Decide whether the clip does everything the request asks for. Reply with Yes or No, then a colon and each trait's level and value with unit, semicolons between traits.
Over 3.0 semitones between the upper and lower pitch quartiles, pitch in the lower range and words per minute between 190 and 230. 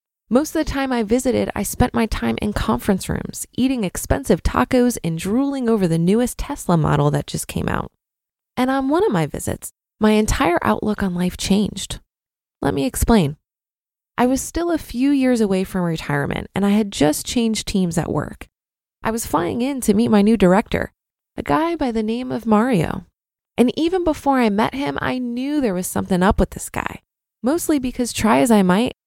No: wide, 5.6 semitones; high, 220 Hz; average, 200 wpm